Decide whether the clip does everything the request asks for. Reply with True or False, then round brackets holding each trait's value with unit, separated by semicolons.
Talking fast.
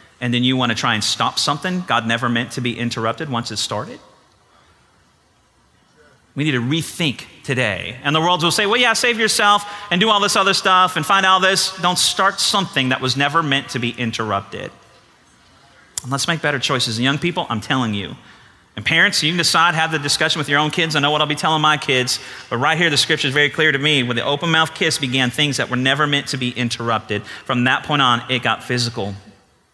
True (230 wpm)